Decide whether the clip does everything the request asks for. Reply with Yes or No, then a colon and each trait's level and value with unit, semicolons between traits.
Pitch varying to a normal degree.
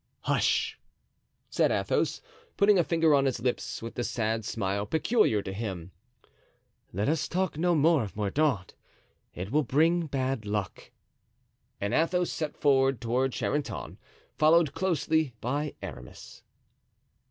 No: wide, 6.8 semitones